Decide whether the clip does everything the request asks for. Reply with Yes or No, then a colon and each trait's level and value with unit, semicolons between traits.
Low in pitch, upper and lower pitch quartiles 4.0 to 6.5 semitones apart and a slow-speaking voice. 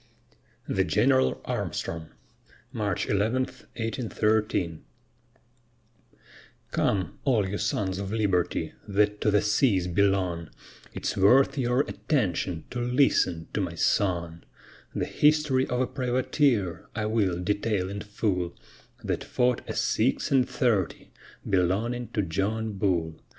Yes: low, 105 Hz; average, 4.9 semitones; slow, 120 wpm